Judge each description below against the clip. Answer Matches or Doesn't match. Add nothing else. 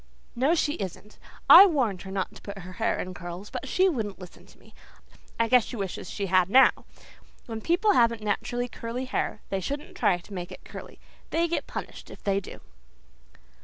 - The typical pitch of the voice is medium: Doesn't match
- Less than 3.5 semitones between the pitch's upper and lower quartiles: Doesn't match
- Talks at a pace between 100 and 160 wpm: Doesn't match